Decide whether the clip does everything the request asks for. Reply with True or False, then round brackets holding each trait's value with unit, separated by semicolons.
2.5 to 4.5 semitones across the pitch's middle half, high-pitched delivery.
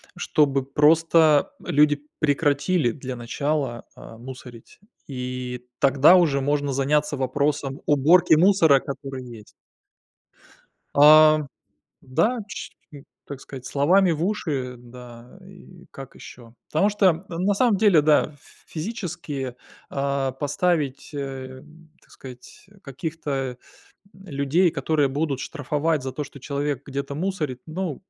False (3.3 semitones; 145 Hz)